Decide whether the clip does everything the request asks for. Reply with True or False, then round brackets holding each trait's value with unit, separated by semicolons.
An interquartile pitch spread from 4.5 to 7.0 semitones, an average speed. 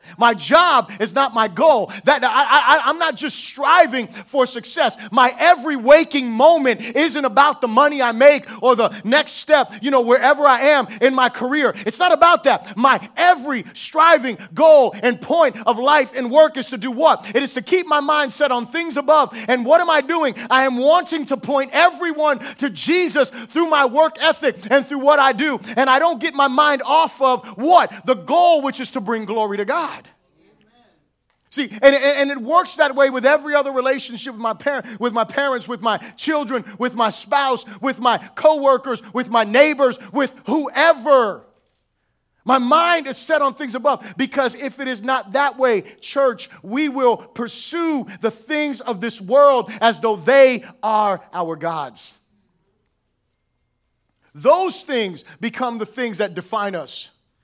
False (3.9 semitones; 175 wpm)